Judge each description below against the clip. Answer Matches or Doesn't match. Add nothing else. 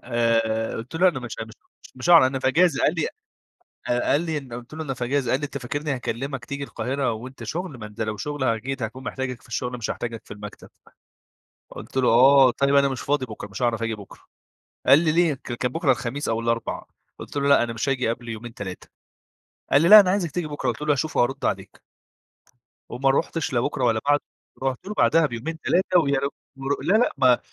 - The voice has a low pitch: Matches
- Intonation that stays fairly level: Doesn't match